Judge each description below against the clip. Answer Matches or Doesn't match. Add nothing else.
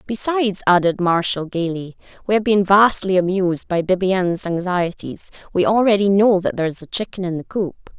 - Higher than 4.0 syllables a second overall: Matches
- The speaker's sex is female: Matches